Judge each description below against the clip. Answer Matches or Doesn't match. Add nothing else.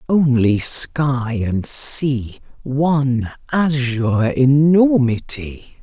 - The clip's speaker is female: Doesn't match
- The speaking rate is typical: Doesn't match